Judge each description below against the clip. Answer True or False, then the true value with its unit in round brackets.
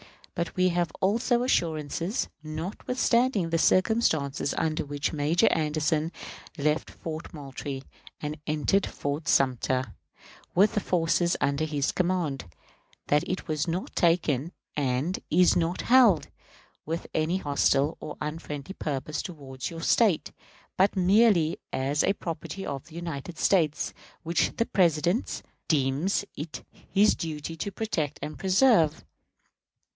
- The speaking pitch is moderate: True (160 Hz)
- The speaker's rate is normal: False (125 wpm)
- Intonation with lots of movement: False (3.8 semitones)